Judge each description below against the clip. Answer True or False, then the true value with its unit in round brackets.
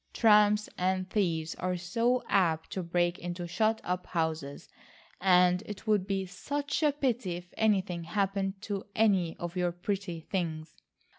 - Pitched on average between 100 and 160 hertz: False (185 Hz)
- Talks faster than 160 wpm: False (150 wpm)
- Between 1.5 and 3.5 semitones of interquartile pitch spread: True (3.1 semitones)